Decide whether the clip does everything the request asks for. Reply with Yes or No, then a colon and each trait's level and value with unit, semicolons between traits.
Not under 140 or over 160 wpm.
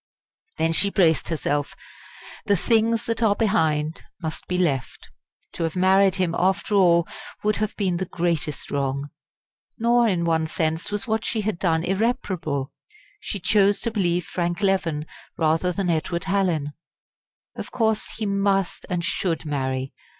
Yes: average, 150 wpm